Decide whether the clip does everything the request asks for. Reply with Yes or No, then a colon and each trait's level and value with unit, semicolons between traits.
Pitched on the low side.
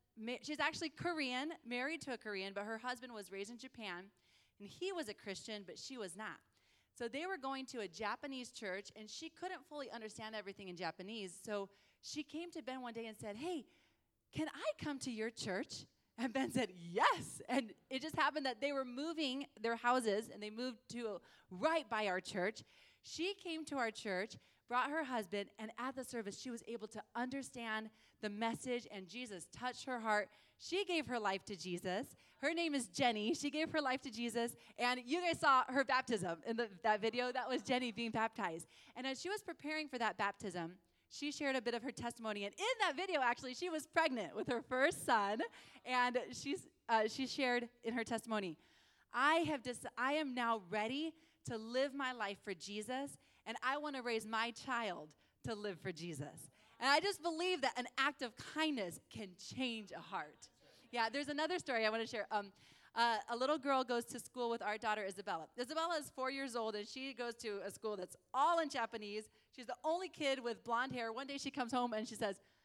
No: high, 245 Hz